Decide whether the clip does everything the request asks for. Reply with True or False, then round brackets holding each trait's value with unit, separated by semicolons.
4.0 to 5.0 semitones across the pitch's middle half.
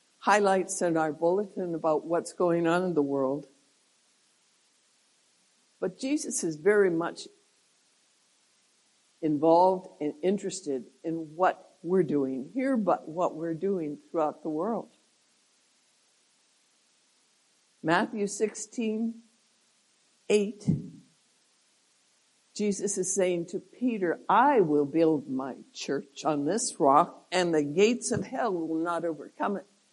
True (4.4 semitones)